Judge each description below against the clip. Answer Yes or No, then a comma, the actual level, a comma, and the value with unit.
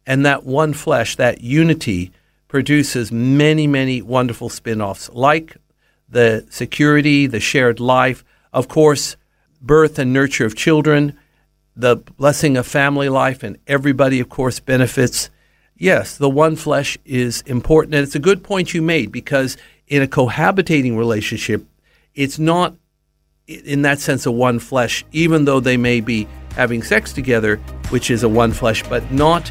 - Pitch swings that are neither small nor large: Yes, average, 3.8 semitones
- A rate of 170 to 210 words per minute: No, average, 155 wpm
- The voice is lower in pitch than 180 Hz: Yes, low, 135 Hz